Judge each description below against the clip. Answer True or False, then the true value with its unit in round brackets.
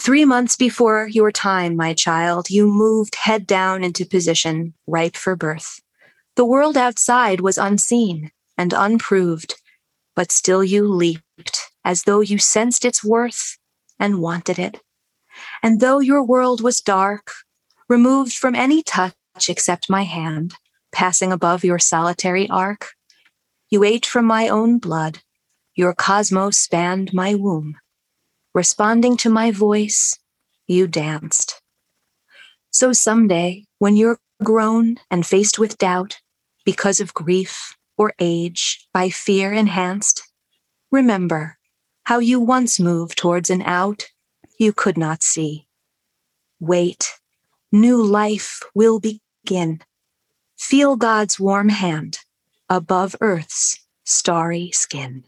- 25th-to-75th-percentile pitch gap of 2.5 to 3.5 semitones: False (4.0 semitones)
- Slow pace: True (125 wpm)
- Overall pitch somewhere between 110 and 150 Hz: False (195 Hz)